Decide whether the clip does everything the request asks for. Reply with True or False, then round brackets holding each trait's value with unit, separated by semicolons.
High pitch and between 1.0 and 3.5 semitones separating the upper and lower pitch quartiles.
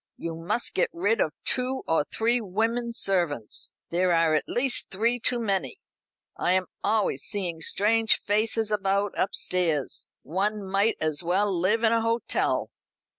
False (200 Hz; 4.4 semitones)